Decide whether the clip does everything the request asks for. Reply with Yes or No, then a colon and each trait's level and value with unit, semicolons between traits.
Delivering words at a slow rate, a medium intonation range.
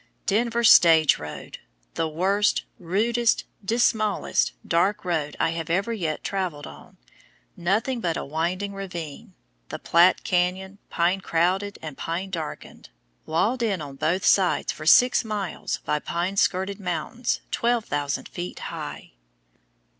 Yes: slow, 125 wpm; average, 3.8 semitones